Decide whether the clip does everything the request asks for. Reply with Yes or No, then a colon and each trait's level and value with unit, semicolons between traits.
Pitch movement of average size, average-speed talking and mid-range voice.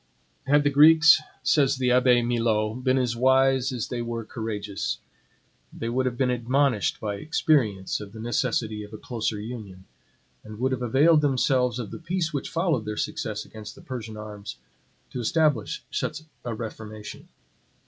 No: average, 3.7 semitones; average, 165 wpm; low, 120 Hz